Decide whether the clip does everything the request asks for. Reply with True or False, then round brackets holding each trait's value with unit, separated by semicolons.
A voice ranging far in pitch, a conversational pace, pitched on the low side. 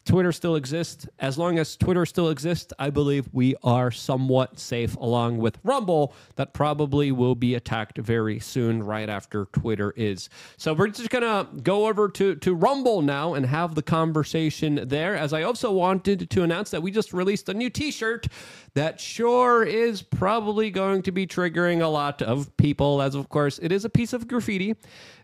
False (6.4 semitones; 190 wpm; 155 Hz)